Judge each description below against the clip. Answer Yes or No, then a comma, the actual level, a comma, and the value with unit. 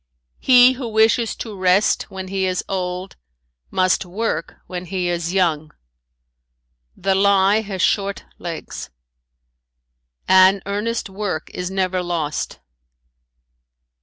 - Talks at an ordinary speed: No, slow, 110 wpm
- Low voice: No, high, 190 Hz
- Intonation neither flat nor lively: No, narrow, 2.1 semitones